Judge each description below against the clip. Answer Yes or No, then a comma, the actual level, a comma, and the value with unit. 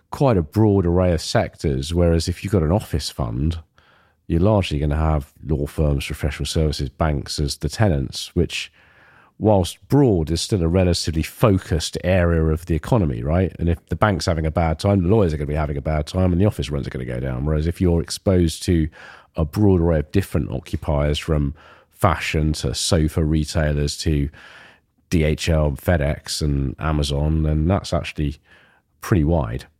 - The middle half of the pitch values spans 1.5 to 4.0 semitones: Yes, average, 3.3 semitones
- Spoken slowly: No, average, 185 wpm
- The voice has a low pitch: Yes, very low, 80 Hz